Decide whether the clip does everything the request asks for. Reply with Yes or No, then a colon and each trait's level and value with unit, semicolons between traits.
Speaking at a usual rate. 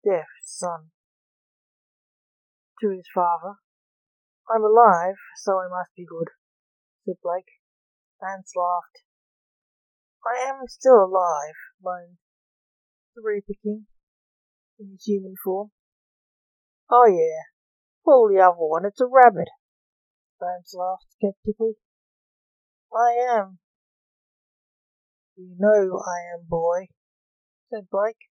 No: slow, 100 wpm